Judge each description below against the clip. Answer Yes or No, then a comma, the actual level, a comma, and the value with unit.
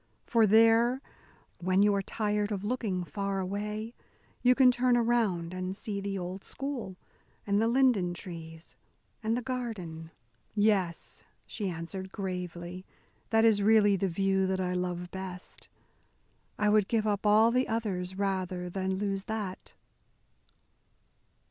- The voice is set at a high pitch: Yes, high, 200 Hz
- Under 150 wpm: Yes, average, 140 wpm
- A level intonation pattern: No, average, 3.2 semitones